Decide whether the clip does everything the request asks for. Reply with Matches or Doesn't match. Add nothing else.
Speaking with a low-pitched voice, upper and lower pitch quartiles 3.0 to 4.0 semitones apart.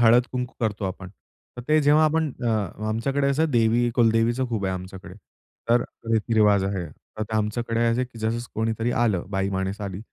Matches